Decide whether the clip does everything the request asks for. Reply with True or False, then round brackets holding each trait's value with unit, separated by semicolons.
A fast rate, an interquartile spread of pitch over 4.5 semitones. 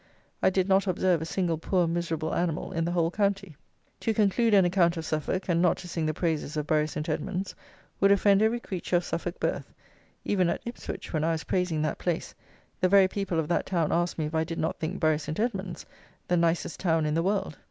False (225 wpm; 2.9 semitones)